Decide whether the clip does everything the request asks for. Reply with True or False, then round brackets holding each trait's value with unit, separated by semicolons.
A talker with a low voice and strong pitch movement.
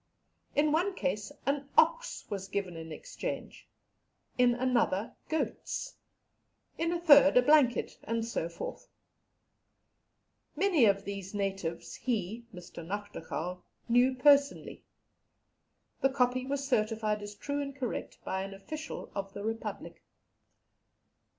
False (235 Hz; 6.1 semitones)